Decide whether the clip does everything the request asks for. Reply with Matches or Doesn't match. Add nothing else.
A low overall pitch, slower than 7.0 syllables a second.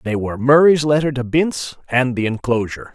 Matches